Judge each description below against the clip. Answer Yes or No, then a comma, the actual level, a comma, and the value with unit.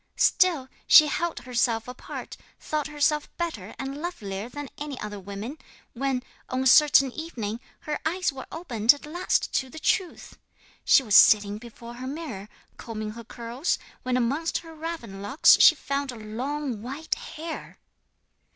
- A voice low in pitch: No, very high, 265 Hz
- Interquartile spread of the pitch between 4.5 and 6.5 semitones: Yes, average, 5.2 semitones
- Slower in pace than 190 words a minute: Yes, average, 150 wpm